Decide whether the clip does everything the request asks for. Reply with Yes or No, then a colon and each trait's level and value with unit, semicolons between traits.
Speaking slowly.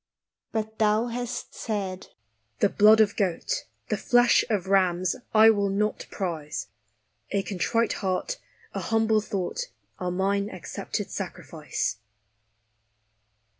Yes: slow, 120 wpm